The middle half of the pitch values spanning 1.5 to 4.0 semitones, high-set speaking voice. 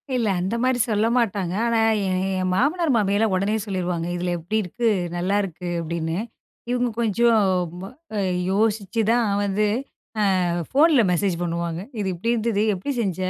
No: average, 4.4 semitones; high, 205 Hz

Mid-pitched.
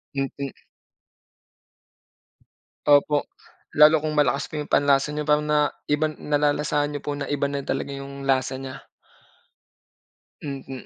Yes: medium, 145 Hz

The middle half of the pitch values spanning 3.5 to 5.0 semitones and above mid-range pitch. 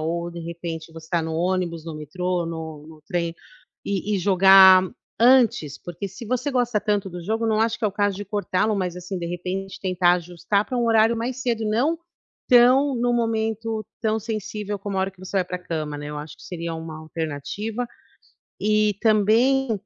Yes: average, 4.6 semitones; high, 195 Hz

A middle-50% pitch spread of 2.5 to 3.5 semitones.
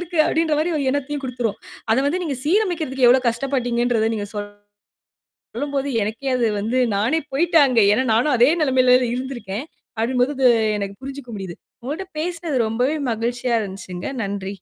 No: average, 4.3 semitones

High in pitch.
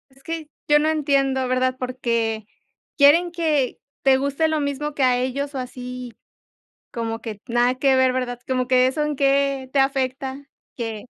Yes: very high, 265 Hz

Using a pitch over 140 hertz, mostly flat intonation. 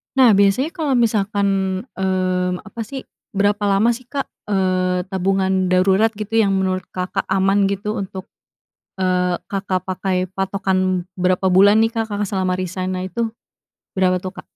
Yes: high, 190 Hz; narrow, 1.8 semitones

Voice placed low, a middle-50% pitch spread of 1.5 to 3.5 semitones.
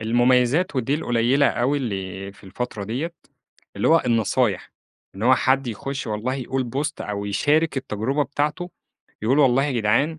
No: low, 125 Hz; average, 4.3 semitones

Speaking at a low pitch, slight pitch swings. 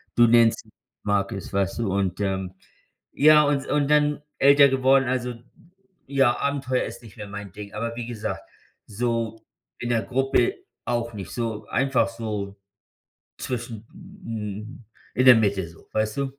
No: low, 115 Hz; average, 4.2 semitones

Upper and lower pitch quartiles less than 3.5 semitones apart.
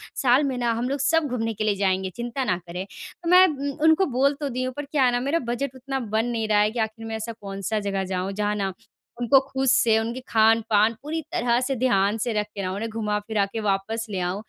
No: average, 4.1 semitones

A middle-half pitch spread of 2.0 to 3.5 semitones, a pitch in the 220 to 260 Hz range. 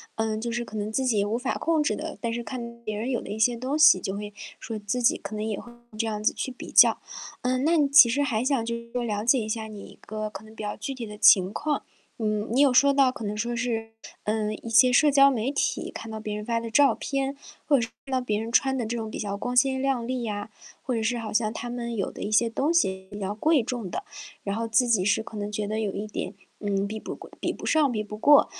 Yes: average, 3.2 semitones; high, 230 Hz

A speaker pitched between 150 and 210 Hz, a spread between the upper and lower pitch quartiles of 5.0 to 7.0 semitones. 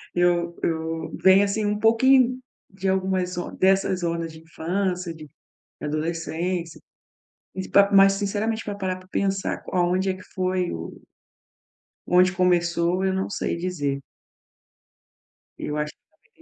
No: medium, 185 Hz; narrow, 2.4 semitones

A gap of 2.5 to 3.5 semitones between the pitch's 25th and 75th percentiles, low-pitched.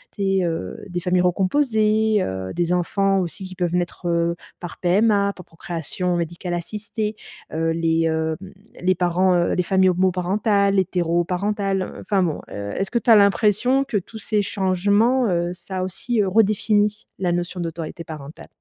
No: average, 3.0 semitones; medium, 185 Hz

